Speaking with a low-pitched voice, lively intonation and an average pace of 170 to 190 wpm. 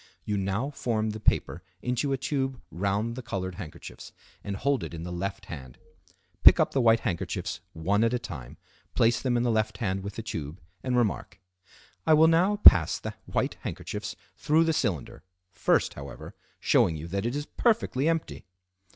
Yes: low, 110 Hz; wide, 5.9 semitones; average, 180 wpm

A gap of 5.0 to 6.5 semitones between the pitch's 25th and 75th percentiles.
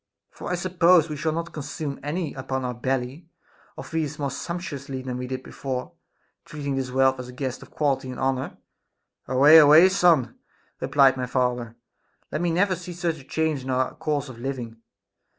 No: average, 3.8 semitones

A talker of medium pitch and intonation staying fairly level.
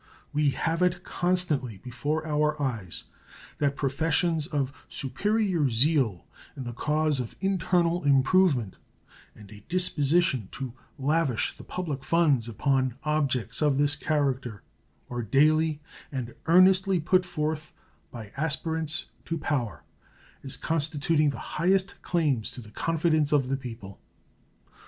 No: medium, 150 Hz; average, 4.1 semitones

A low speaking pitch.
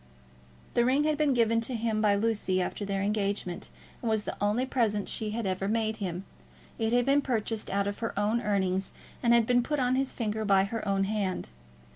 No: high, 215 Hz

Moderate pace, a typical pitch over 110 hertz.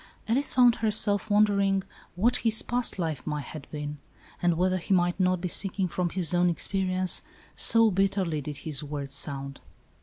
Yes: average, 170 wpm; medium, 185 Hz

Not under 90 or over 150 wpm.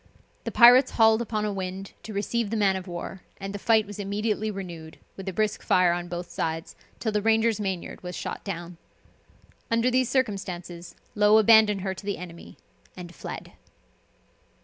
No: average, 175 wpm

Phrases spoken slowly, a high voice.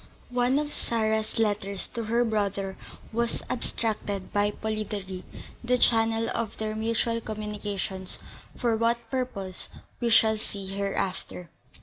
Yes: slow, 120 wpm; high, 220 Hz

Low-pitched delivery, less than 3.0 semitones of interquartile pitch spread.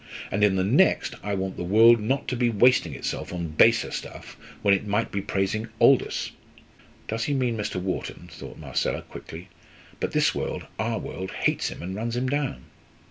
No: low, 110 Hz; average, 3.7 semitones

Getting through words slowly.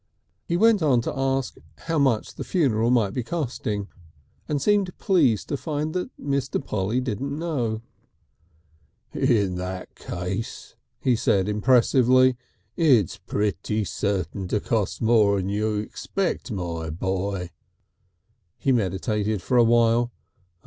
Yes: slow, 120 wpm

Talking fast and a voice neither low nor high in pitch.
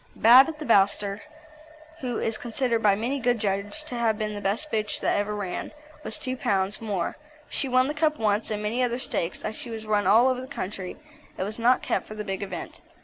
No: fast, 225 wpm; high, 220 Hz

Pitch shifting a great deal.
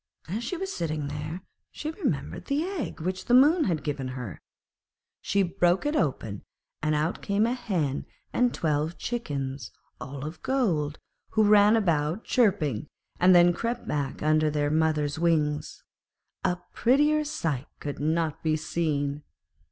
Yes: wide, 7.1 semitones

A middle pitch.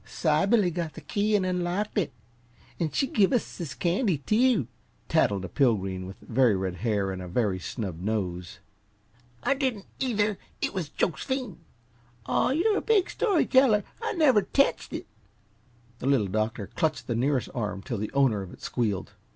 Yes: medium, 150 Hz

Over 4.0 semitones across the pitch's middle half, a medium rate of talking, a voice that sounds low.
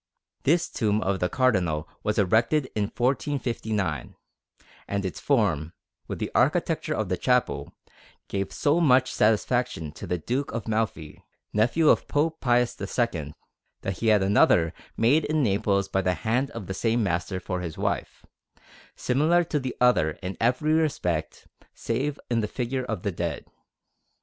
Yes: wide, 5.5 semitones; average, 155 wpm; low, 110 Hz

